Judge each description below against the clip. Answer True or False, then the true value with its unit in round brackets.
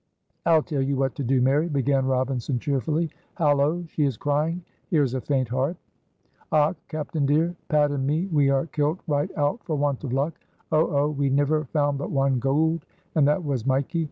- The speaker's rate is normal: True (195 wpm)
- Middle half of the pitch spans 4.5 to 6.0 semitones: False (2.4 semitones)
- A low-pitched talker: False (145 Hz)